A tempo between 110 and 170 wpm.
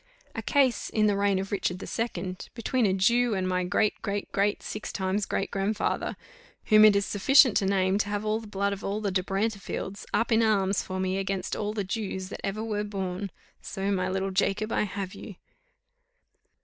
No: fast, 205 wpm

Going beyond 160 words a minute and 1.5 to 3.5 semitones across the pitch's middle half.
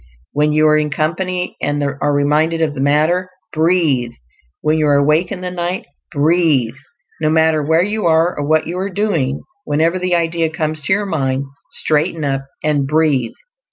Yes: average, 180 wpm; average, 2.9 semitones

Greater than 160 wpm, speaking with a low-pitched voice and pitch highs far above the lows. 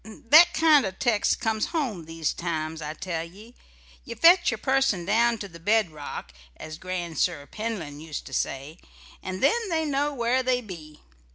No: average, 170 wpm; high, 195 Hz; wide, 7.7 semitones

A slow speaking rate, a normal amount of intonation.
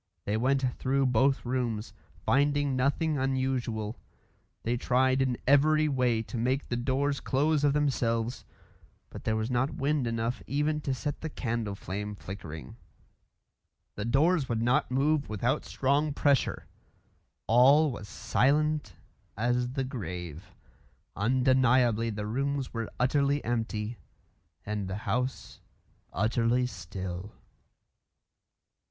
Yes: slow, 120 wpm; average, 3.7 semitones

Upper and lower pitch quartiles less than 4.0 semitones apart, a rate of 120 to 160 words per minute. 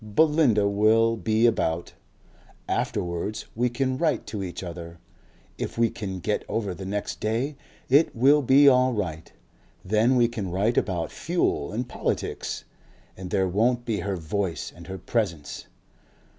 No: average, 4.5 semitones; average, 150 wpm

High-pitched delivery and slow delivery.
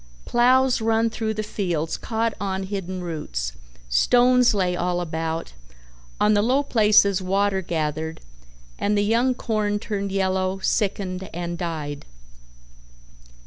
Yes: high, 195 Hz; slow, 125 wpm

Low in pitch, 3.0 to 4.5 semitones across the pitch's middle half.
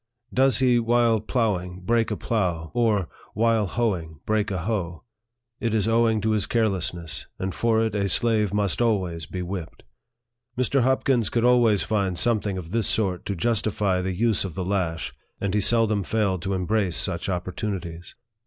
Yes: low, 105 Hz; average, 3.8 semitones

